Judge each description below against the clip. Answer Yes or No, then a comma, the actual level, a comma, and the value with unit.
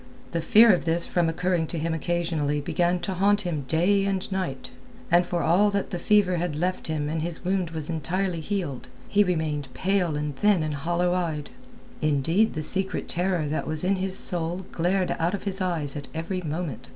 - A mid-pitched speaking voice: Yes, medium, 175 Hz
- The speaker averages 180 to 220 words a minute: Yes, average, 200 wpm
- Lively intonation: No, average, 3.0 semitones